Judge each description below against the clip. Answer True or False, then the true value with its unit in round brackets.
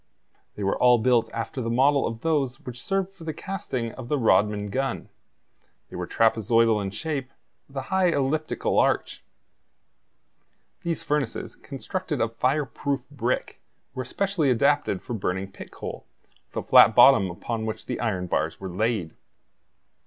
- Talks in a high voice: False (125 Hz)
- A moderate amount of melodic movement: True (4.7 semitones)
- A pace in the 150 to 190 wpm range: True (155 wpm)